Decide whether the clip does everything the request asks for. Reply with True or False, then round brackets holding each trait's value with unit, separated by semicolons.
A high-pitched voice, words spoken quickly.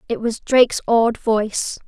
False (230 Hz; 160 wpm)